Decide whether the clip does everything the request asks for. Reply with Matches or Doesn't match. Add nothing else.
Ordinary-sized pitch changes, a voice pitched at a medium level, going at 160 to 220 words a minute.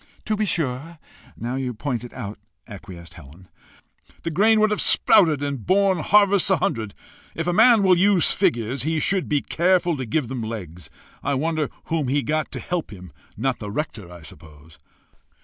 Doesn't match